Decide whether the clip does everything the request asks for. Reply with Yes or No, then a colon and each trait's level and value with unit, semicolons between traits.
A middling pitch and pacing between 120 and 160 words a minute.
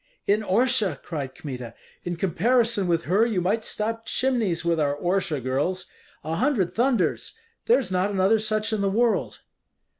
No: high, 195 Hz; average, 155 wpm